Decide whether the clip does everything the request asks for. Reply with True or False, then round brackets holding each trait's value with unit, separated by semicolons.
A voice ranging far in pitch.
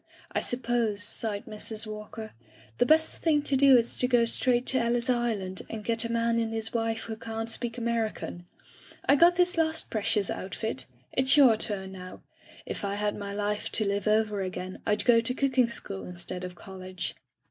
False (2.9 semitones)